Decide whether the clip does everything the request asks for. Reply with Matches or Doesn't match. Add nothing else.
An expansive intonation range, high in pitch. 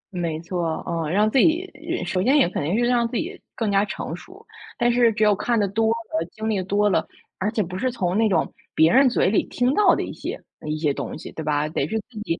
Matches